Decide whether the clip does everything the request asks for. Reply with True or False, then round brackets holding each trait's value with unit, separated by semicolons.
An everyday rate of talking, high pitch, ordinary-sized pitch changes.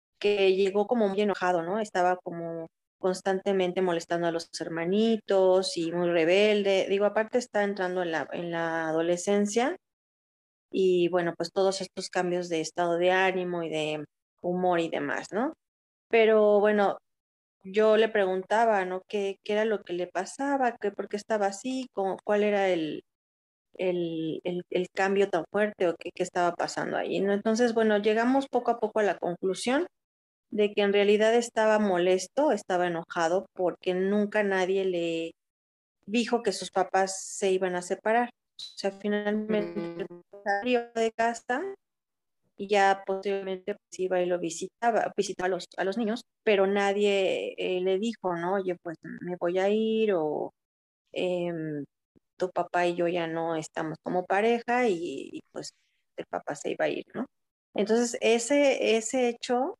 True (160 wpm; 195 Hz; 3.3 semitones)